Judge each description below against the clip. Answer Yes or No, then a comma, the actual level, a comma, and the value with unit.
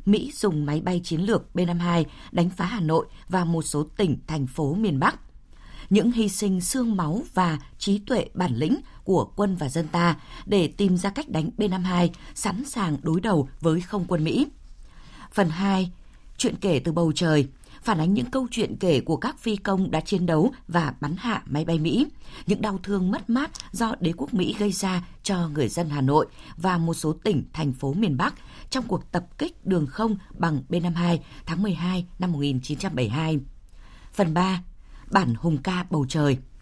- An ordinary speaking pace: Yes, average, 190 wpm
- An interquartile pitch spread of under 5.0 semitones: Yes, average, 4.3 semitones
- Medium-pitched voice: Yes, medium, 175 Hz